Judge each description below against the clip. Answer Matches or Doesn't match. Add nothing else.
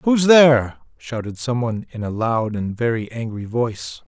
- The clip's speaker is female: Doesn't match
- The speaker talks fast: Doesn't match